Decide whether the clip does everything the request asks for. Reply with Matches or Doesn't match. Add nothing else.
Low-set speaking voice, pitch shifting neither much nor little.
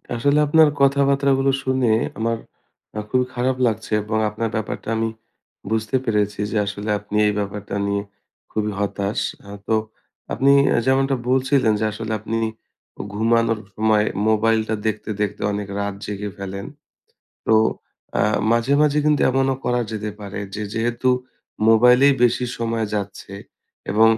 Matches